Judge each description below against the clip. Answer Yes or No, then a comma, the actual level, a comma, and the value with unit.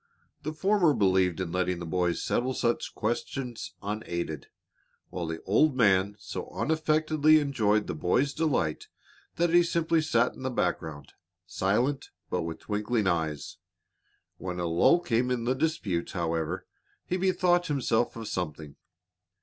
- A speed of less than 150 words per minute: Yes, average, 140 wpm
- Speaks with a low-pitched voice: Yes, low, 115 Hz